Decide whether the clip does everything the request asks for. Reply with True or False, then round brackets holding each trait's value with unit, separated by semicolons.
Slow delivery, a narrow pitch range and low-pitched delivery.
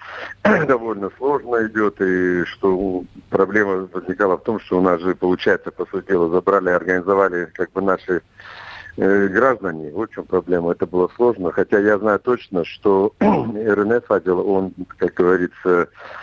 False (145 wpm; 2.3 semitones; 95 Hz)